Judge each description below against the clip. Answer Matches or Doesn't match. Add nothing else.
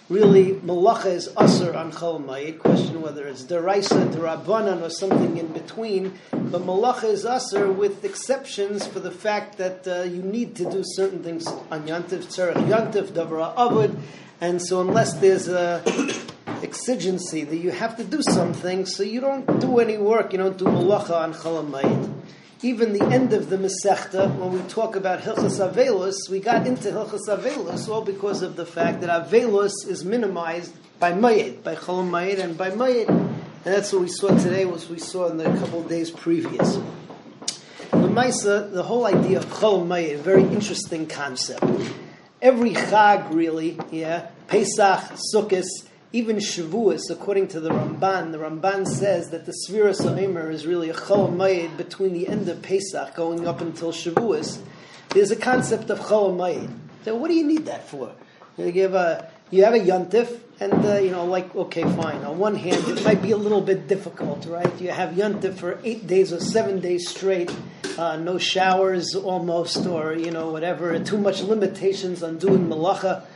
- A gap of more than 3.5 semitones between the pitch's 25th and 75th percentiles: Doesn't match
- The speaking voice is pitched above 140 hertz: Matches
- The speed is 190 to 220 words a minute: Doesn't match